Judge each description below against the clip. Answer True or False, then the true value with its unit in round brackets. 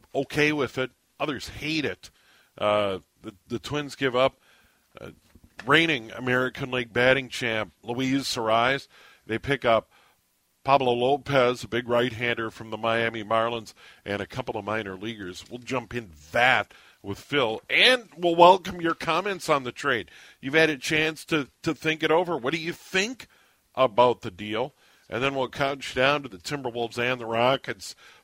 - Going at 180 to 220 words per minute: False (170 wpm)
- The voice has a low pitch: True (125 Hz)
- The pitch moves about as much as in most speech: True (4.3 semitones)